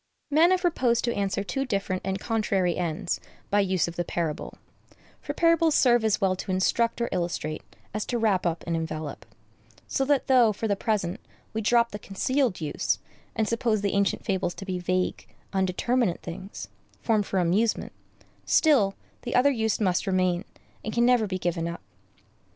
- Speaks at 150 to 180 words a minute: Yes, average, 175 wpm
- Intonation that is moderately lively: Yes, average, 4.3 semitones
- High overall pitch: Yes, high, 200 Hz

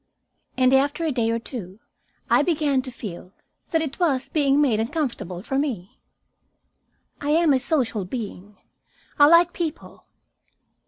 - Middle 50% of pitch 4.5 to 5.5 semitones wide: Yes, average, 5.1 semitones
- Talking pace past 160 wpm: No, average, 145 wpm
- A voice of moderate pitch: No, very high, 270 Hz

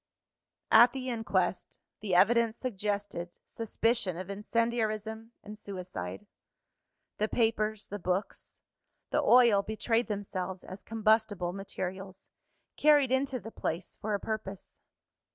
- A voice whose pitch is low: No, high, 215 Hz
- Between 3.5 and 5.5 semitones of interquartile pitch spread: No, average, 3.1 semitones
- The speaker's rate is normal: No, slow, 115 wpm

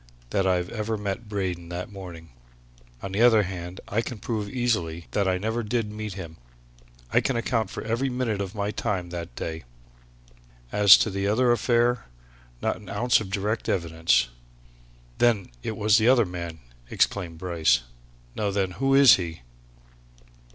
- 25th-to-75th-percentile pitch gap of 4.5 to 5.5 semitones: No, average, 4.1 semitones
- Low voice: Yes, low, 100 Hz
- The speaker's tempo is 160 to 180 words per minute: Yes, average, 165 wpm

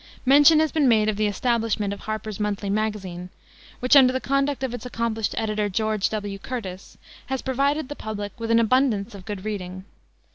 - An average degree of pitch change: Yes, average, 3.8 semitones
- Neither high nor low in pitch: No, high, 220 Hz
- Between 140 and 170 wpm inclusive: No, average, 185 wpm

